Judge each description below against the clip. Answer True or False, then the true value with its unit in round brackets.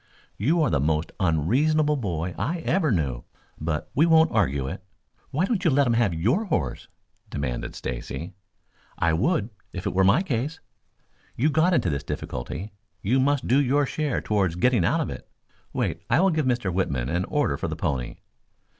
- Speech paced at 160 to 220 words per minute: True (180 wpm)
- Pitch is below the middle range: True (110 Hz)